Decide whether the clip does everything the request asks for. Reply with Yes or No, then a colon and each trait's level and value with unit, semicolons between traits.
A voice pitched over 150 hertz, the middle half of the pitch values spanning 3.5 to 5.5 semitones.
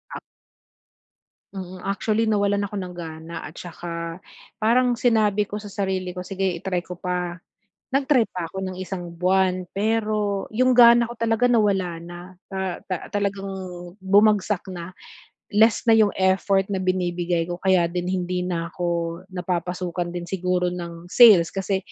No: medium, 185 Hz; average, 2.7 semitones